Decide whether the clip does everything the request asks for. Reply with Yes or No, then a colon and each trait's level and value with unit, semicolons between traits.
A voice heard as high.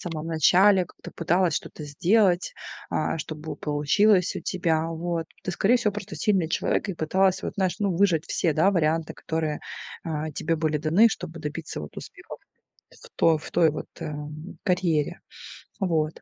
No: medium, 165 Hz